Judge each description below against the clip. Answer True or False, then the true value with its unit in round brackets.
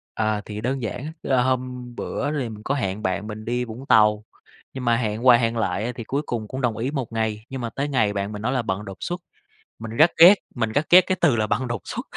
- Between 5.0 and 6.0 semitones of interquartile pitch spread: False (3.3 semitones)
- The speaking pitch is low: True (115 Hz)